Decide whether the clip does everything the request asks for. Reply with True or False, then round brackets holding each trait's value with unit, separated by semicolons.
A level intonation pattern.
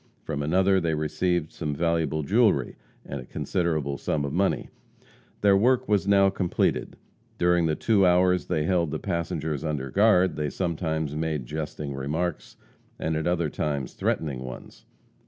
False (3.5 semitones)